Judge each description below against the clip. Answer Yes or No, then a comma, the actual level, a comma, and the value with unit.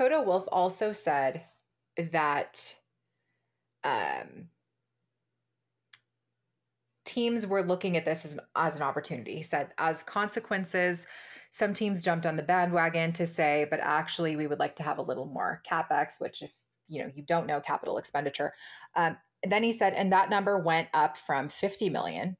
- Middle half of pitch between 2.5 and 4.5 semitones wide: No, average, 4.9 semitones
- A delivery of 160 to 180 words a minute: Yes, average, 165 wpm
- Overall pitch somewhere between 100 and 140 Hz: No, medium, 165 Hz